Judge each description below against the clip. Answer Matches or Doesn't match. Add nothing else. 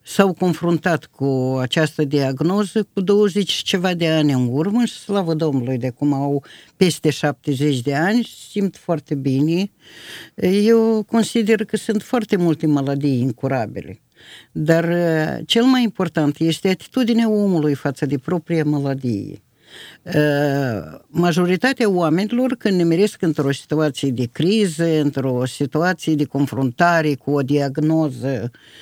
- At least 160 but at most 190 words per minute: Doesn't match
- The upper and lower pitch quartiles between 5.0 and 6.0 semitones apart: Matches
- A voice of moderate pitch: Matches